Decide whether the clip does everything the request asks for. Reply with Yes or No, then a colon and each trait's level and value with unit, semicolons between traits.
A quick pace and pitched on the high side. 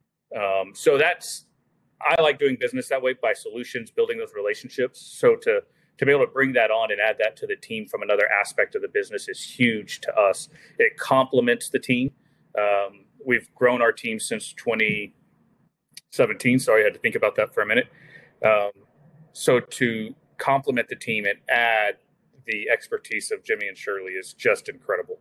No: average, 185 wpm; high, 225 Hz